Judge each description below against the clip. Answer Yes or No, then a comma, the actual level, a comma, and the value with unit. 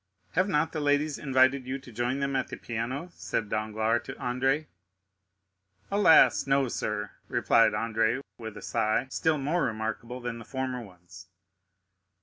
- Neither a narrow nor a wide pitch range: Yes, average, 3.7 semitones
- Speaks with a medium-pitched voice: No, low, 125 Hz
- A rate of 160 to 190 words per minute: No, average, 150 wpm